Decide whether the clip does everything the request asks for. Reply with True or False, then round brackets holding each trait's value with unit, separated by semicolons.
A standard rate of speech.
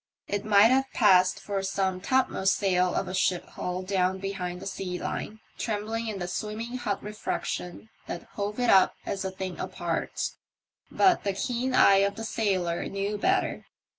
True (170 wpm)